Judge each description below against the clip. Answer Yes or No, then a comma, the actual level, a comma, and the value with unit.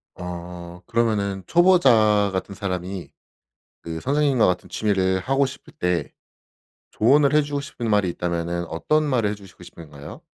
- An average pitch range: No, wide, 6.5 semitones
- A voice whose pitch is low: Yes, low, 100 Hz